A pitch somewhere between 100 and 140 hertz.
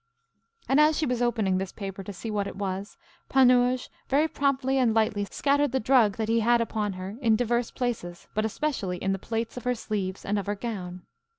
No: high, 225 Hz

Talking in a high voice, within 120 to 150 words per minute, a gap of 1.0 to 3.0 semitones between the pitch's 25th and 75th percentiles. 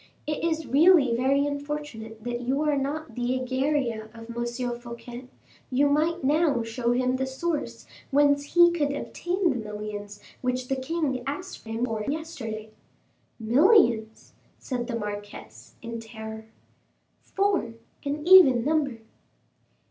No: very high, 255 Hz; slow, 135 wpm; average, 4.4 semitones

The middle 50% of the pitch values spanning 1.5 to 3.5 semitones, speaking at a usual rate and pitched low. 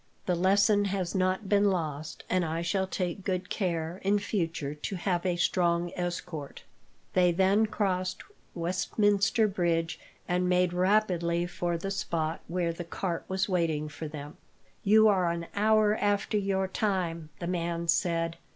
No: narrow, 2.5 semitones; average, 150 wpm; medium, 180 Hz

